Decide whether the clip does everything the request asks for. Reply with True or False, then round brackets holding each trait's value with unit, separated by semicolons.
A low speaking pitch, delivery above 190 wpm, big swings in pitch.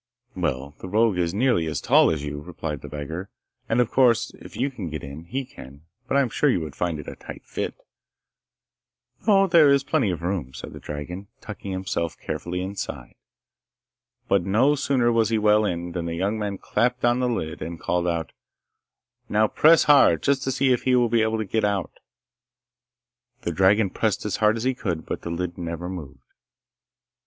True (100 Hz; 200 wpm; 6.0 semitones)